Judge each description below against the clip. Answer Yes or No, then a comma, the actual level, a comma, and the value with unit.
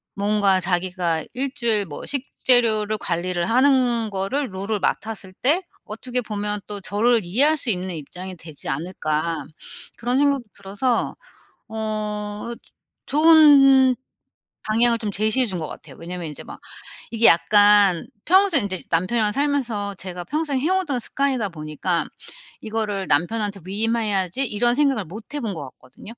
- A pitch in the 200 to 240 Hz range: Yes, high, 210 Hz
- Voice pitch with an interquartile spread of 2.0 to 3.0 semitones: No, average, 5.1 semitones